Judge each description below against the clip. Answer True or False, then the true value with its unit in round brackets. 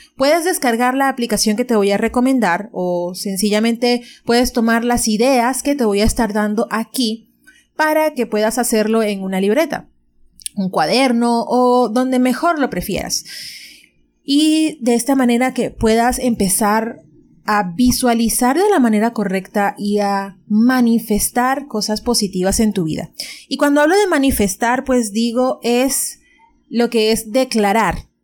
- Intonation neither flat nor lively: True (3.4 semitones)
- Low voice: False (235 Hz)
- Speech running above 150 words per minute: False (145 wpm)